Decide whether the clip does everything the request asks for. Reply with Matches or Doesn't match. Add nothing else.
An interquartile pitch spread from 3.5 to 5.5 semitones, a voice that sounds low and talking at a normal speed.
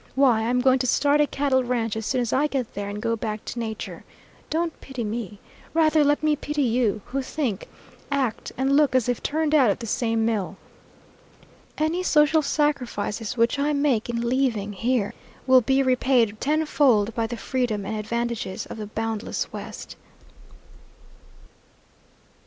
Doesn't match